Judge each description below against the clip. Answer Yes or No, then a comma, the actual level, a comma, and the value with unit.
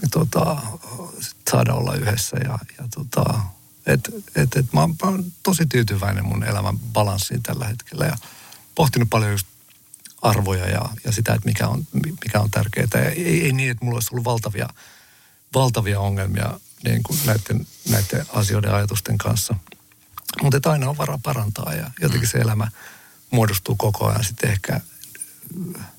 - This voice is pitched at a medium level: No, low, 120 Hz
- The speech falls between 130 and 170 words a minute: Yes, fast, 155 wpm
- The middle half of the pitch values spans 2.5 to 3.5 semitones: No, average, 4.9 semitones